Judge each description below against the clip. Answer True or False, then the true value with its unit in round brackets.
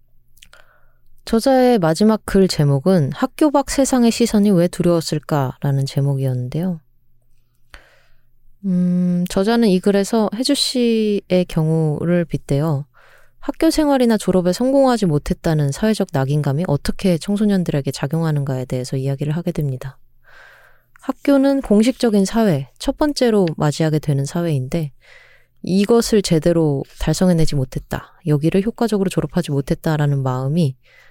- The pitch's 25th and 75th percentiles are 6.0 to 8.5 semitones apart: True (7.2 semitones)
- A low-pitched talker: False (175 Hz)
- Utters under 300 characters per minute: False (310 characters per minute)